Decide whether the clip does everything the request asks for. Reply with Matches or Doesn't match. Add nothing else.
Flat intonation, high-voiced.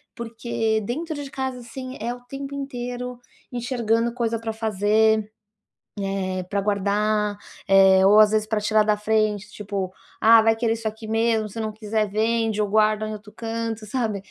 Matches